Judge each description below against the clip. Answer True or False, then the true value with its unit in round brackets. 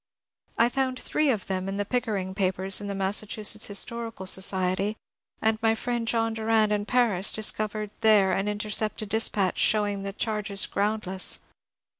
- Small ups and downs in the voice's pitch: True (2.2 semitones)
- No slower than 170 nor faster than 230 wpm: False (150 wpm)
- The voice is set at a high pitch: True (210 Hz)